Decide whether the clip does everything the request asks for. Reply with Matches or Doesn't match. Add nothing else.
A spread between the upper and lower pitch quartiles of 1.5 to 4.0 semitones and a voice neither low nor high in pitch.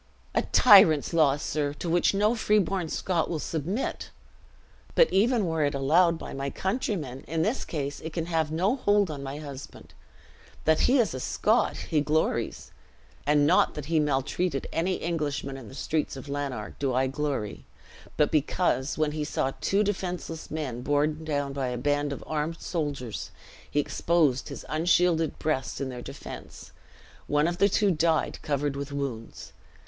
Matches